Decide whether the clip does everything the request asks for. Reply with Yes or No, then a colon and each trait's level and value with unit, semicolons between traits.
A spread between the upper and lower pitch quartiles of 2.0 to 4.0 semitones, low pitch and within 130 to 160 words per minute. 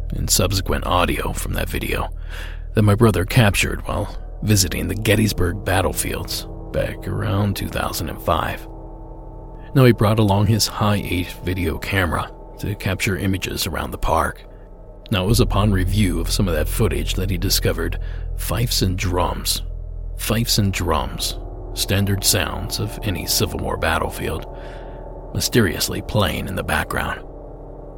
Yes: average, 3.4 semitones; very low, 95 Hz; average, 140 wpm